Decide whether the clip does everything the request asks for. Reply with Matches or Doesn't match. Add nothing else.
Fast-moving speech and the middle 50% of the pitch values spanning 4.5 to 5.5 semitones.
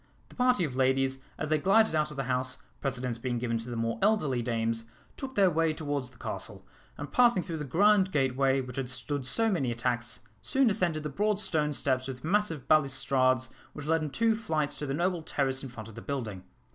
Matches